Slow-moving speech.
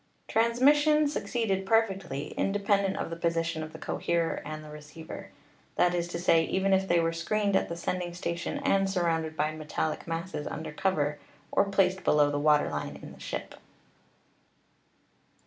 No: average, 165 wpm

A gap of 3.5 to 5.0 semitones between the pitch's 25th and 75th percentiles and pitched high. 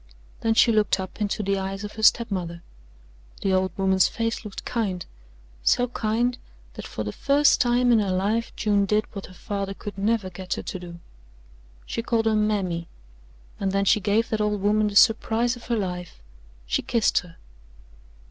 No: average, 3.1 semitones; high, 205 Hz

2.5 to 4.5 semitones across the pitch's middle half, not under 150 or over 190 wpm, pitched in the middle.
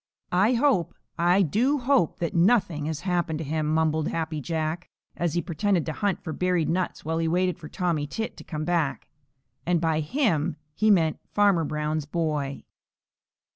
Yes: average, 2.8 semitones; average, 175 wpm; medium, 165 Hz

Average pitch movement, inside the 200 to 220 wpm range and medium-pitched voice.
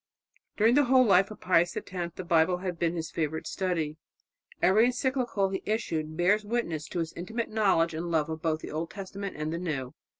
Yes: average, 4.4 semitones; fast, 205 wpm; medium, 180 Hz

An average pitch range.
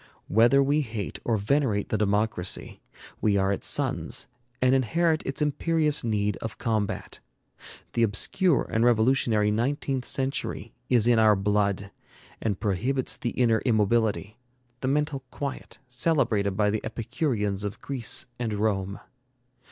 Yes: average, 4.5 semitones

